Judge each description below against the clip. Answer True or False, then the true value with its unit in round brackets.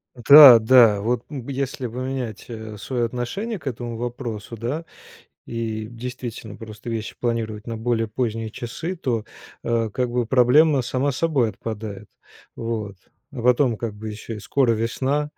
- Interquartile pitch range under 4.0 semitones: True (2.7 semitones)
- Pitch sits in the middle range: False (120 Hz)